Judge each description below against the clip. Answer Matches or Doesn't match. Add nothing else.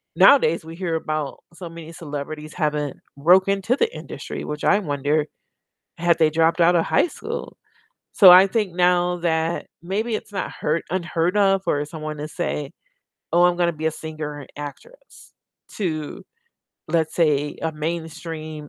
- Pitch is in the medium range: Matches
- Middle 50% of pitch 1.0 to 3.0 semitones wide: Matches